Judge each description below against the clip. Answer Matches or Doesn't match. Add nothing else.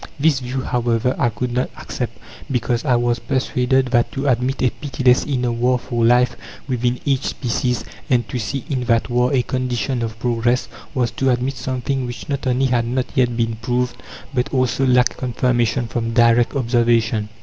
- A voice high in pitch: Doesn't match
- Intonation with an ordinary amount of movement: Doesn't match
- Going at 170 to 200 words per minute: Matches